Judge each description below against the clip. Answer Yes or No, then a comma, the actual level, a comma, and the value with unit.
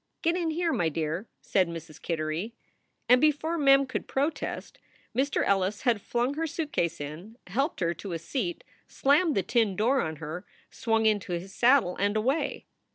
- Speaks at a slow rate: No, average, 170 wpm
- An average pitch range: No, wide, 8.1 semitones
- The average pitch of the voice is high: Yes, high, 220 Hz